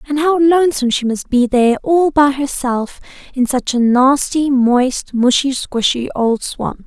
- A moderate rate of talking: Yes, average, 165 wpm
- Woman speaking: Yes, female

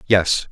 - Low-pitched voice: Yes, very low, 90 Hz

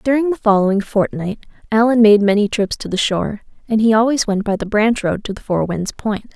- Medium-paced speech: No, fast, 215 wpm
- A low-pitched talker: No, high, 210 Hz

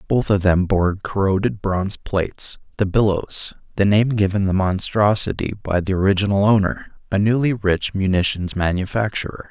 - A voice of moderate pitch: No, low, 100 Hz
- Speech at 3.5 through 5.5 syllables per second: Yes, 5.0 syllables/s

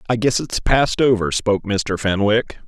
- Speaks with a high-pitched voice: No, low, 110 Hz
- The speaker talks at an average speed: Yes, average, 180 wpm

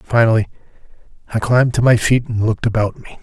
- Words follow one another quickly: No, average, 185 wpm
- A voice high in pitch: No, low, 115 Hz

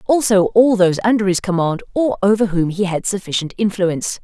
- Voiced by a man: No, female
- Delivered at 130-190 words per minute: Yes, average, 185 wpm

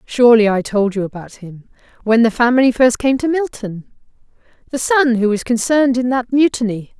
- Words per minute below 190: Yes, average, 170 wpm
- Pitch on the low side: No, high, 235 Hz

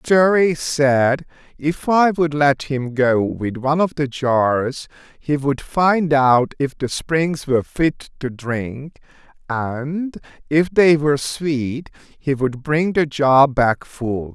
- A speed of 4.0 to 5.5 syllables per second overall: No, 3.2 syllables/s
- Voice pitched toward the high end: No, medium, 145 Hz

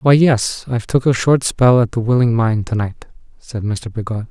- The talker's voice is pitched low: Yes, low, 120 Hz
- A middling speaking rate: No, fast, 210 wpm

